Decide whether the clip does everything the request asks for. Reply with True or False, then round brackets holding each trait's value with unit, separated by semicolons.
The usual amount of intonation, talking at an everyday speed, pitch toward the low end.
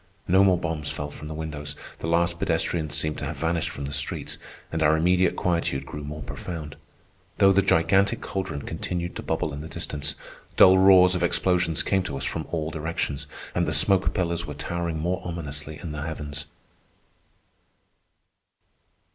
True (3.1 semitones; 170 wpm; 80 Hz)